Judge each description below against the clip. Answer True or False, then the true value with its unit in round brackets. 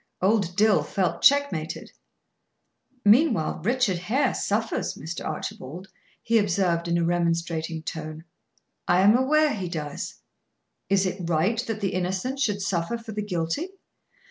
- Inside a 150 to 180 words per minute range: False (135 wpm)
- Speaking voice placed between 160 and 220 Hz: True (190 Hz)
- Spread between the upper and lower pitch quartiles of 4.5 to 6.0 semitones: True (4.8 semitones)